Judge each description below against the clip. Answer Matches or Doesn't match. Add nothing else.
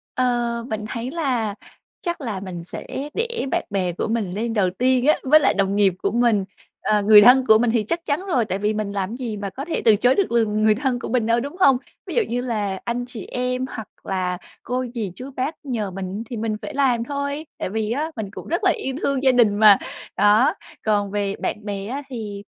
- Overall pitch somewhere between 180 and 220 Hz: Doesn't match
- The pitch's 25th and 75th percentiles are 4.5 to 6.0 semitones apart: Doesn't match